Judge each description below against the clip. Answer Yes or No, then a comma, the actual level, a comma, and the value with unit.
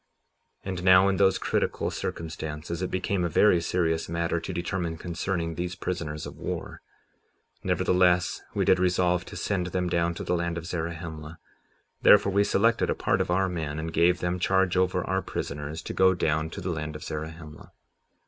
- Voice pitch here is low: Yes, very low, 85 Hz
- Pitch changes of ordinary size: No, narrow, 2.1 semitones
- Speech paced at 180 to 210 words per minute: Yes, average, 185 wpm